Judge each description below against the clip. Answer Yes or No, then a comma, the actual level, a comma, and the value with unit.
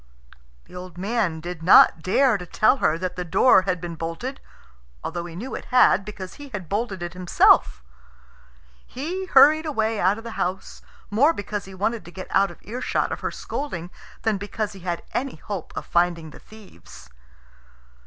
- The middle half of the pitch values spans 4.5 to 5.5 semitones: Yes, average, 4.8 semitones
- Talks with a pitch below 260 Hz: Yes, high, 190 Hz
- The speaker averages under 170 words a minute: No, average, 185 wpm